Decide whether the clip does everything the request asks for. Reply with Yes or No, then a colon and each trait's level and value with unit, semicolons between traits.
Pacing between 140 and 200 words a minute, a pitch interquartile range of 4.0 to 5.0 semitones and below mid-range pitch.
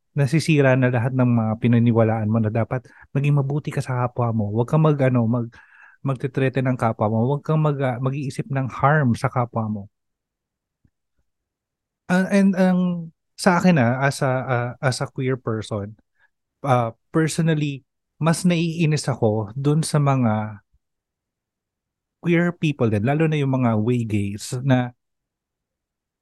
Yes: average, 150 wpm; average, 4.5 semitones; low, 130 Hz